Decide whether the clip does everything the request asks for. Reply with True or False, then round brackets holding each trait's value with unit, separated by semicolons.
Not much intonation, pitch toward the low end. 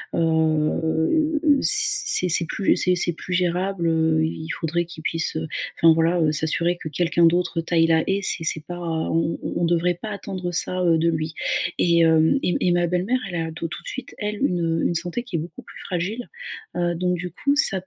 False (1.9 semitones; 170 Hz)